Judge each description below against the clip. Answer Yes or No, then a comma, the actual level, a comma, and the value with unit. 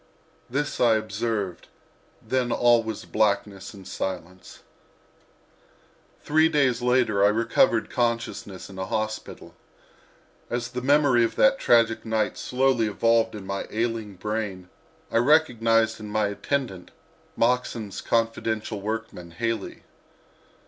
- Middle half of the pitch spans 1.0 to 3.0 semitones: Yes, narrow, 2.6 semitones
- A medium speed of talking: No, slow, 115 wpm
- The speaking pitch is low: Yes, low, 115 Hz